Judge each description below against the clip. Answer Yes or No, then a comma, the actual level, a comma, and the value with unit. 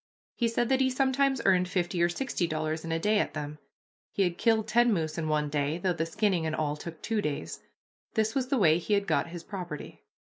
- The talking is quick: Yes, fast, 235 wpm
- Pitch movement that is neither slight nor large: No, wide, 5.8 semitones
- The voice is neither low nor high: Yes, medium, 175 Hz